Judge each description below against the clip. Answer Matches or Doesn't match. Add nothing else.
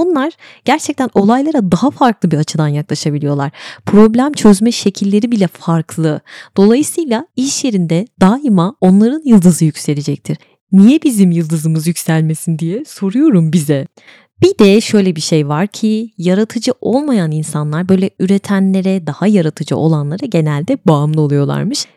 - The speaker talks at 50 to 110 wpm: Doesn't match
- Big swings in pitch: Matches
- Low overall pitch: Doesn't match